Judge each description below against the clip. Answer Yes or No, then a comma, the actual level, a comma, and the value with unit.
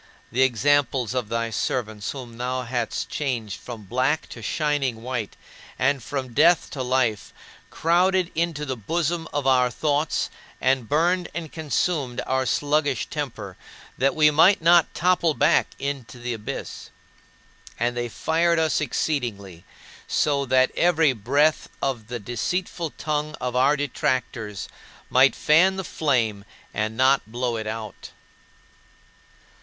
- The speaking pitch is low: Yes, low, 130 Hz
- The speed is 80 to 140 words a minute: Yes, slow, 135 wpm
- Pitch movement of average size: Yes, average, 4.3 semitones